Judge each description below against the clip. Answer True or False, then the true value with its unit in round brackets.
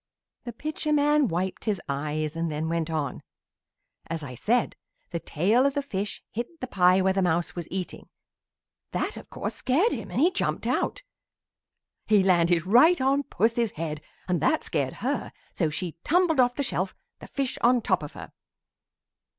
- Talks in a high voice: True (195 Hz)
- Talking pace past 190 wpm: False (175 wpm)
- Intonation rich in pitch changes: True (7.6 semitones)